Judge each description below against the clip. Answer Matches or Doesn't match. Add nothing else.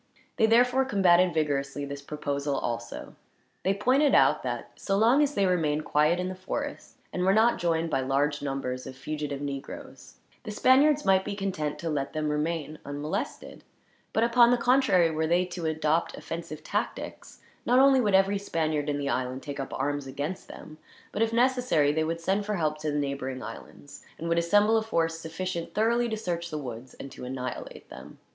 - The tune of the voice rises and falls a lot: Matches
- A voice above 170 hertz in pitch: Doesn't match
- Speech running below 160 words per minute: Doesn't match